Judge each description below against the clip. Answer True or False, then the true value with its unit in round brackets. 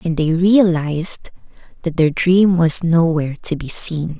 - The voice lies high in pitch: False (165 Hz)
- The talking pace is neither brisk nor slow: True (155 wpm)